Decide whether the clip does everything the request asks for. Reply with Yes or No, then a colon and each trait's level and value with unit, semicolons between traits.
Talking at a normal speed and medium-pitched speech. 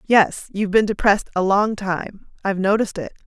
No: average, 180 wpm; high, 200 Hz